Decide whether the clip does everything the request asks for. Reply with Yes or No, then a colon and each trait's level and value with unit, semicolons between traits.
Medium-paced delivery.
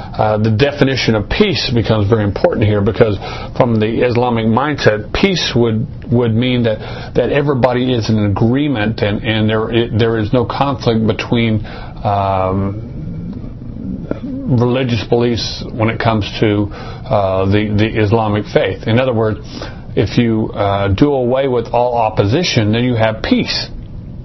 Yes: average, 150 wpm